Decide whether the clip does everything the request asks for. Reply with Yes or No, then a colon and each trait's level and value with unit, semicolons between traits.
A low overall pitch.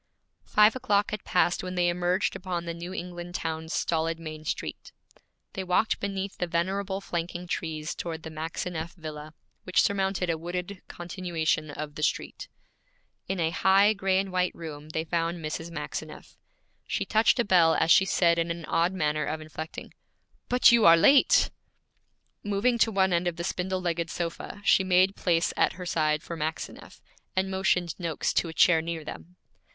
No: medium, 175 Hz